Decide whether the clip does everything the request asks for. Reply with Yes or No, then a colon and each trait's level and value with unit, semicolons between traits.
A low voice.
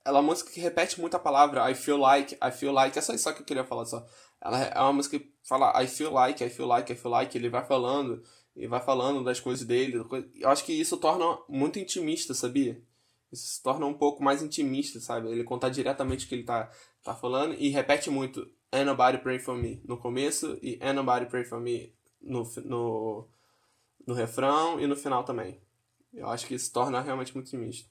Yes: low, 130 Hz